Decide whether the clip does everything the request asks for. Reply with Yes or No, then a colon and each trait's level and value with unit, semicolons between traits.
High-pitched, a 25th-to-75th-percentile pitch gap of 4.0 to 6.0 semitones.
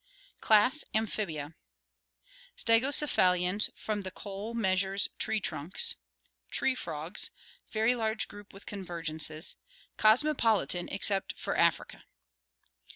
No: high, 205 Hz; average, 3.5 semitones